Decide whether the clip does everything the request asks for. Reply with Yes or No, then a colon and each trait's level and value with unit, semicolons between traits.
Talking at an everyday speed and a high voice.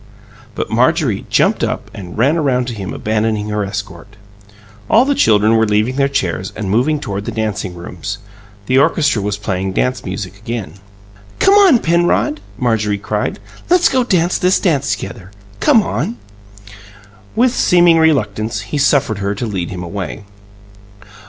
No: average, 150 wpm; low, 110 Hz